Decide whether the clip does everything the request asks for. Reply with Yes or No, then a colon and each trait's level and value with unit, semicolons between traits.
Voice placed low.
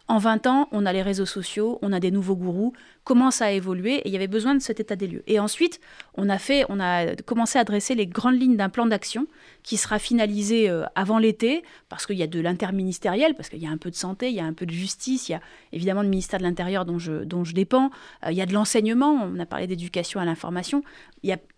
No: high, 205 Hz